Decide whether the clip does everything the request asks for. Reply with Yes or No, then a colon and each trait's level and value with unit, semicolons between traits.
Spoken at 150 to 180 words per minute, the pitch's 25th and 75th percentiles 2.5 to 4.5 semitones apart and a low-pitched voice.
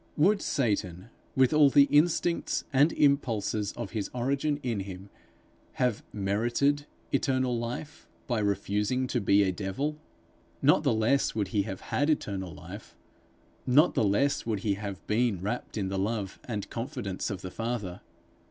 No: average, 155 wpm; wide, 5.4 semitones; low, 115 Hz